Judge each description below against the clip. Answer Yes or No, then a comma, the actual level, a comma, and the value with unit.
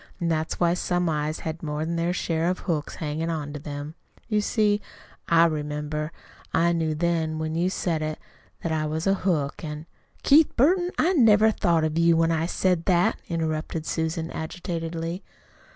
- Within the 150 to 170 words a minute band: No, average, 185 wpm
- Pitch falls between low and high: Yes, medium, 165 Hz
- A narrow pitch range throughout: Yes, narrow, 2.1 semitones